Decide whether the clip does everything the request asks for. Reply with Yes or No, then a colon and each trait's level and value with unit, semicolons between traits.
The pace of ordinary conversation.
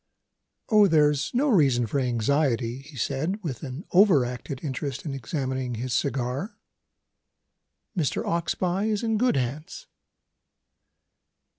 No: slow, 120 wpm